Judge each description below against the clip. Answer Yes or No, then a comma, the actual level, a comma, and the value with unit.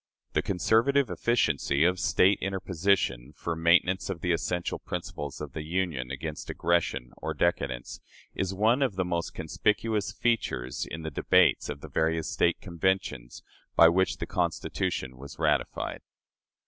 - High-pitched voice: No, very low, 85 Hz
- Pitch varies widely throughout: No, average, 3.9 semitones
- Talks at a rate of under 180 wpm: Yes, average, 145 wpm